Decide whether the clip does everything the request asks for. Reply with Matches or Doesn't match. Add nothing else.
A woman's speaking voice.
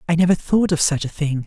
Doesn't match